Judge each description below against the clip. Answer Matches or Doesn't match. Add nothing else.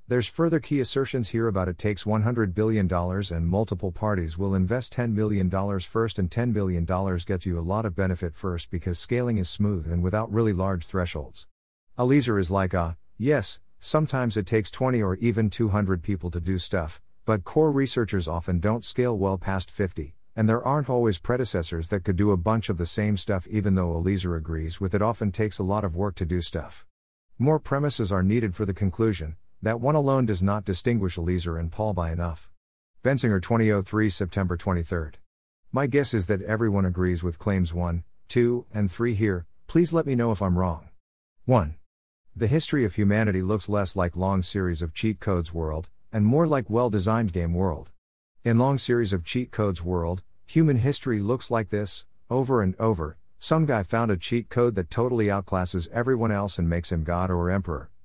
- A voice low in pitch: Matches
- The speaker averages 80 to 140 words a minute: Doesn't match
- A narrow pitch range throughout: Doesn't match